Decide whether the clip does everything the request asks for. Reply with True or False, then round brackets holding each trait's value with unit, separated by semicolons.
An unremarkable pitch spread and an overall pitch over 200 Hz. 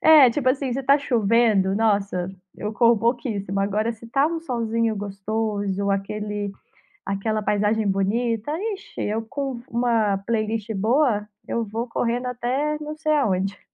True (3.3 semitones; 225 Hz)